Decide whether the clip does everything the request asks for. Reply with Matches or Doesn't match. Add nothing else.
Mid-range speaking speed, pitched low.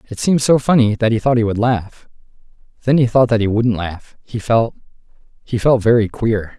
Matches